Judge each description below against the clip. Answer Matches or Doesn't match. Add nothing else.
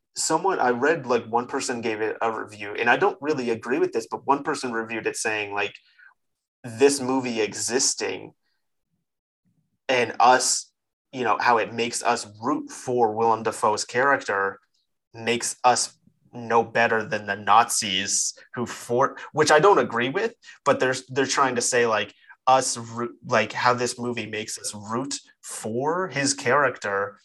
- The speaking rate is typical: Matches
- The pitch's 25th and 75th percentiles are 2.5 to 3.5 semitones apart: Matches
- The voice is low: Matches